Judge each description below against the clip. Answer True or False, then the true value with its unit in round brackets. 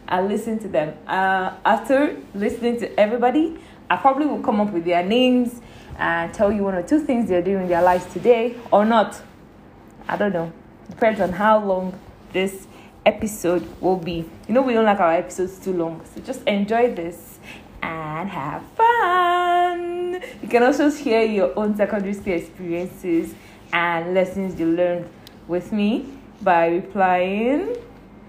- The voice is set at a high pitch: True (200 Hz)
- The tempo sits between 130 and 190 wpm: True (160 wpm)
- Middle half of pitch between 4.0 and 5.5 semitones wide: True (5.1 semitones)